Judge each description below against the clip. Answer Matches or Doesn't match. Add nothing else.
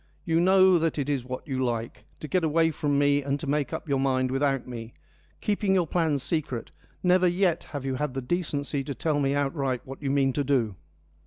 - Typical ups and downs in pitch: Matches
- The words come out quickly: Matches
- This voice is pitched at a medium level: Matches